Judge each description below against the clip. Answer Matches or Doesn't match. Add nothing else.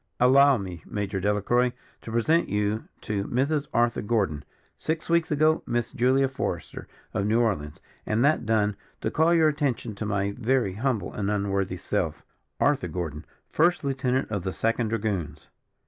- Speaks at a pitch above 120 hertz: Doesn't match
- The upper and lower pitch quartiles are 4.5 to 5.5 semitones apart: Matches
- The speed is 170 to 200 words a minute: Doesn't match